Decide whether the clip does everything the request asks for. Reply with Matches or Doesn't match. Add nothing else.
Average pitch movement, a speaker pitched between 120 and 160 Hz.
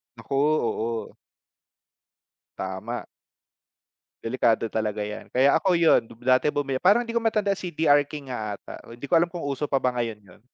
Doesn't match